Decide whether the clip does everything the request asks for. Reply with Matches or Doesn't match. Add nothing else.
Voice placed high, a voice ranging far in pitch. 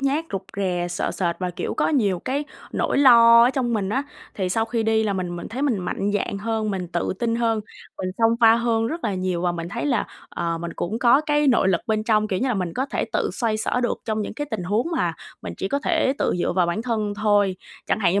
Doesn't match